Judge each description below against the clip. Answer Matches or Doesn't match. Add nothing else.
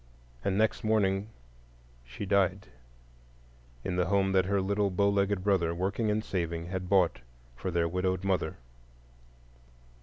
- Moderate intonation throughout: Doesn't match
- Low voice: Matches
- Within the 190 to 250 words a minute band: Doesn't match